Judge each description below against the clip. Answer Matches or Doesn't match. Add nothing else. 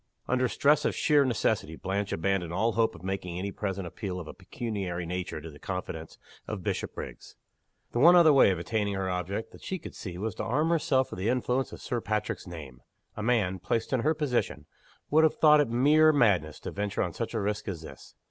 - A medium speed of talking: Doesn't match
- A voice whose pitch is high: Doesn't match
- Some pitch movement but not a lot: Doesn't match